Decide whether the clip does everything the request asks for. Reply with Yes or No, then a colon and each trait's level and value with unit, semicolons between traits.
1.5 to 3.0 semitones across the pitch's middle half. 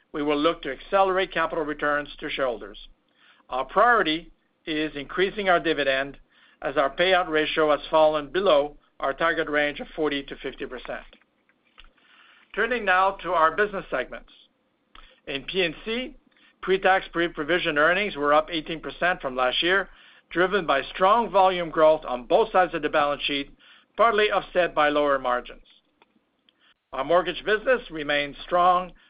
No: average, 4.2 semitones